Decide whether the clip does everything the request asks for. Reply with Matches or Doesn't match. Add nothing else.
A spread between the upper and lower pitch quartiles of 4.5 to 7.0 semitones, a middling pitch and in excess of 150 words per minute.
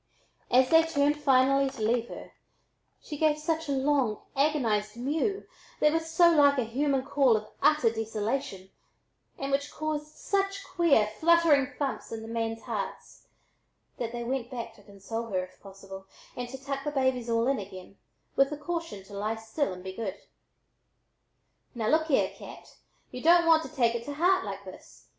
Doesn't match